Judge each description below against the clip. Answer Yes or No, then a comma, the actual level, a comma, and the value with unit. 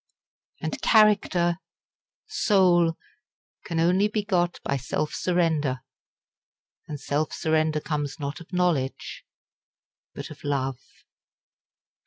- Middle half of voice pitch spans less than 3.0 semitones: No, average, 3.7 semitones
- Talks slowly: Yes, slow, 105 wpm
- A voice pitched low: No, medium, 165 Hz